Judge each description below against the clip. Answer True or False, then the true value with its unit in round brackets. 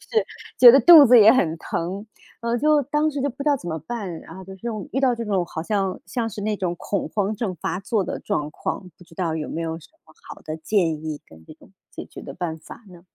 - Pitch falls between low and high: False (195 Hz)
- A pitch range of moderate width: False (6.1 semitones)